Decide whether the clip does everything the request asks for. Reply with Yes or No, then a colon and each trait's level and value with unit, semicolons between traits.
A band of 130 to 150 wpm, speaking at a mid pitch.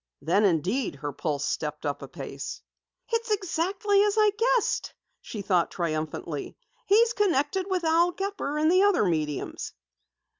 No: average, 145 wpm; very high, 300 Hz